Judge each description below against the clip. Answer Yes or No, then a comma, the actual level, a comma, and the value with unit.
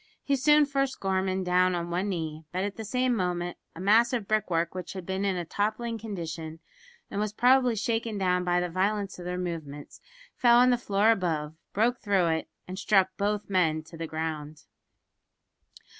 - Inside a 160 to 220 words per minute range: Yes, average, 190 wpm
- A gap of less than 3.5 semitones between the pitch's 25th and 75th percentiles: No, average, 3.9 semitones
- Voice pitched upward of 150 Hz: Yes, high, 190 Hz